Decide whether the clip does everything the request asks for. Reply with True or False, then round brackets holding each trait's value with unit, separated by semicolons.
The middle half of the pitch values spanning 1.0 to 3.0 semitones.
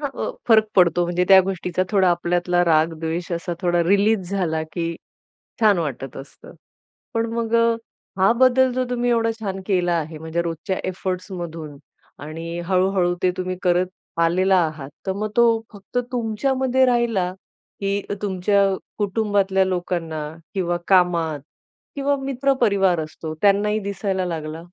False (3.6 semitones)